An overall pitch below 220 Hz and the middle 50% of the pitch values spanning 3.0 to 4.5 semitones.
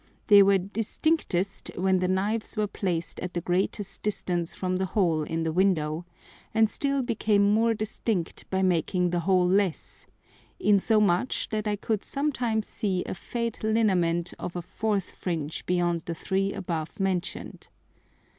Yes: high, 190 Hz; average, 3.3 semitones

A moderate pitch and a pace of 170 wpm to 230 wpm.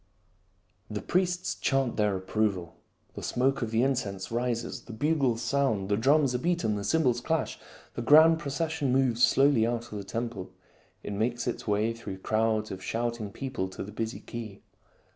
No: low, 120 Hz; average, 175 wpm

